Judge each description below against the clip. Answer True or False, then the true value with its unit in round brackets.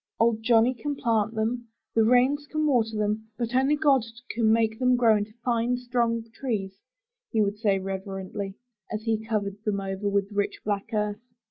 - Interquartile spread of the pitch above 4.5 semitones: False (2.8 semitones)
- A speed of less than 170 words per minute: False (175 wpm)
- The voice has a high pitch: True (220 Hz)